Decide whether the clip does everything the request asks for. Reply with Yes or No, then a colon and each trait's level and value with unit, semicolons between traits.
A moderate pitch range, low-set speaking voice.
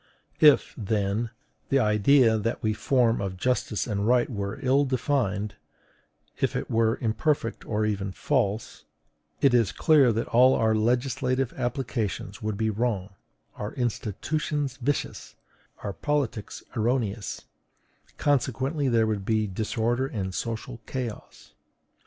Yes: average, 3.4 semitones; low, 115 Hz